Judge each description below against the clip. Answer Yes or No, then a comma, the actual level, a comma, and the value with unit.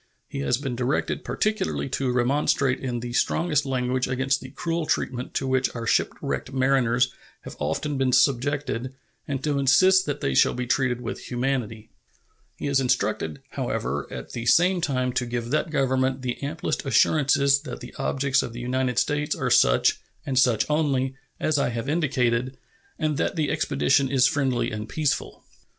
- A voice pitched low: Yes, low, 130 Hz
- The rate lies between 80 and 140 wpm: No, average, 170 wpm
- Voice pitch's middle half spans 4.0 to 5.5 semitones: No, narrow, 2.6 semitones